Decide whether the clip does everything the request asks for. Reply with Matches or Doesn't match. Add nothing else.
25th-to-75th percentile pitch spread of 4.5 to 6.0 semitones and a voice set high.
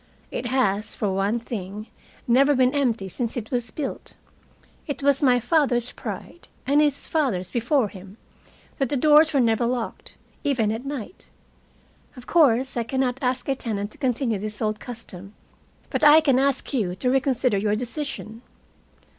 Doesn't match